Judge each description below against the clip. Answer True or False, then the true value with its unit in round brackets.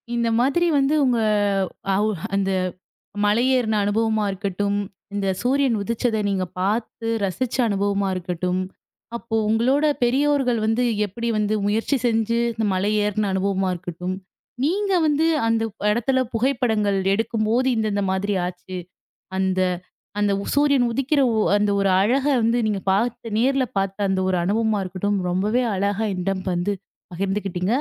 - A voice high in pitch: True (215 Hz)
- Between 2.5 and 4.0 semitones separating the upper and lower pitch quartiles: True (3.5 semitones)